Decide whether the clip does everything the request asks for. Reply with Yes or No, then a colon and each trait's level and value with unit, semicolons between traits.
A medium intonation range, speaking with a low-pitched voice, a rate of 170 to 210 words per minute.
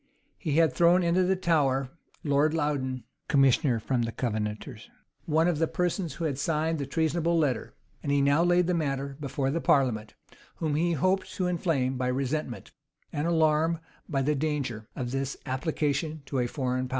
No: average, 3.7 semitones; medium, 145 Hz; average, 180 wpm